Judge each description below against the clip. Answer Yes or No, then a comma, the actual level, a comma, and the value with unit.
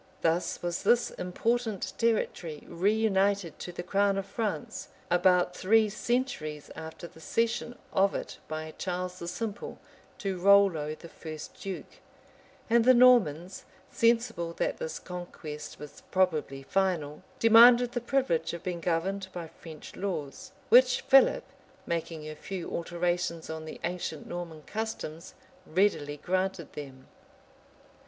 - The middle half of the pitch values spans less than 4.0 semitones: No, average, 4.7 semitones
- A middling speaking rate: No, slow, 130 wpm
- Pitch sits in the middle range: Yes, medium, 180 Hz